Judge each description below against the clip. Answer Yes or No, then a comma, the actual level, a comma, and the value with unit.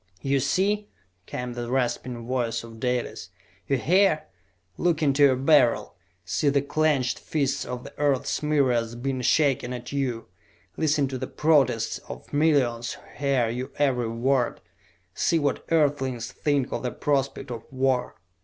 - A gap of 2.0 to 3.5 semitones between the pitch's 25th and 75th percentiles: Yes, average, 3.0 semitones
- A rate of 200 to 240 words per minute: No, average, 155 wpm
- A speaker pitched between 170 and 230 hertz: No, low, 135 Hz